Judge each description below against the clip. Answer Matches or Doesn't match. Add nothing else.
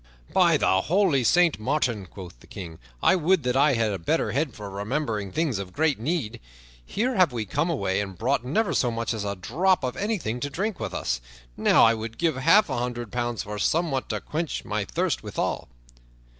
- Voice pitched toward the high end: Doesn't match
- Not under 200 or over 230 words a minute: Matches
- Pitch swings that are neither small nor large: Doesn't match